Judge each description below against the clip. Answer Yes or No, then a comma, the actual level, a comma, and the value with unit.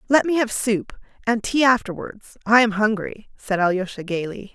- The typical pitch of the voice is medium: No, high, 215 Hz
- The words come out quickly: No, average, 170 wpm